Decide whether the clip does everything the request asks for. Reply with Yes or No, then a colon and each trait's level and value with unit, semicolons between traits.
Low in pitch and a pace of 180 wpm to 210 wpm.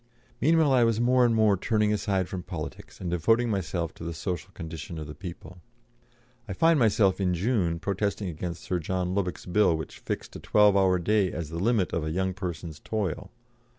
Yes: very low, 95 Hz; average, 195 wpm